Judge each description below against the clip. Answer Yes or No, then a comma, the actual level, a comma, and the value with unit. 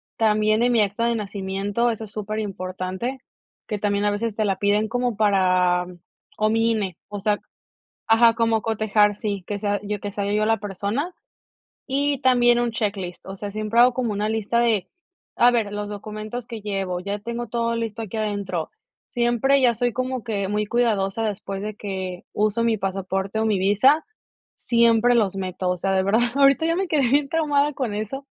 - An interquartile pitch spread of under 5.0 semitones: Yes, average, 2.8 semitones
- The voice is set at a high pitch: Yes, high, 215 Hz